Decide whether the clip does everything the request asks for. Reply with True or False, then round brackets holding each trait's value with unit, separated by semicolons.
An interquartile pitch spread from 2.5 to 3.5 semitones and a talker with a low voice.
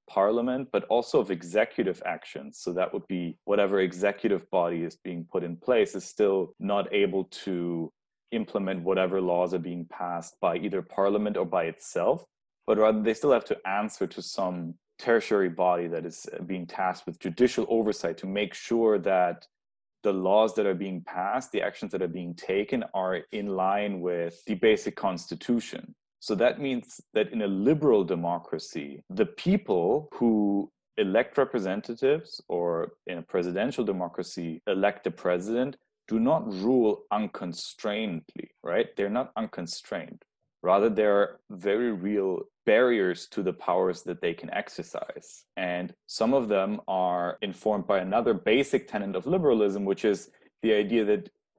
True (3.0 semitones; 95 Hz)